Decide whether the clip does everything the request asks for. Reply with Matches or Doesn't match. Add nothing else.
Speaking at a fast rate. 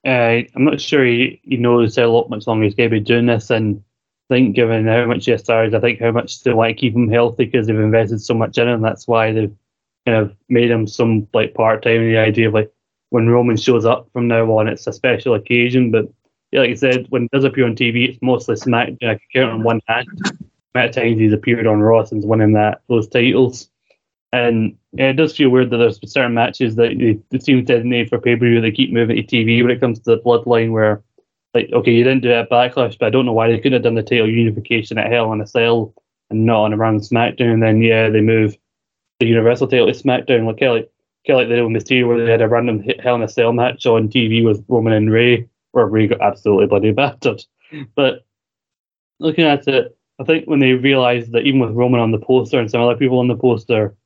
Matches